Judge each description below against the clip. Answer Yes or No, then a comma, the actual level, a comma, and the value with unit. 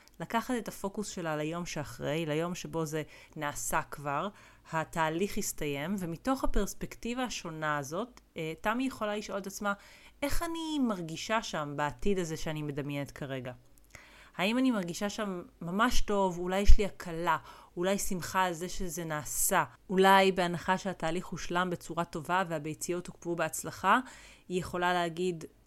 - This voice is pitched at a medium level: Yes, medium, 180 Hz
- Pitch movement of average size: Yes, average, 4.0 semitones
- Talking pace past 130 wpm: Yes, average, 140 wpm